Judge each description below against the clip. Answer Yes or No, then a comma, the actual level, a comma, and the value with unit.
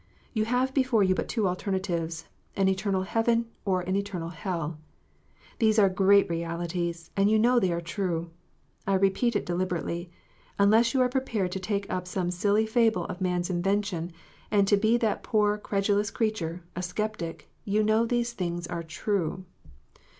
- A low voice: No, high, 195 Hz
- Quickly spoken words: No, average, 170 wpm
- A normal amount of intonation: Yes, average, 3.6 semitones